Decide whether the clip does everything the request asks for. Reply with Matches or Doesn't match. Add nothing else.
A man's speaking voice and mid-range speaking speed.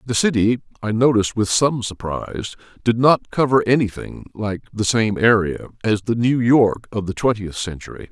Matches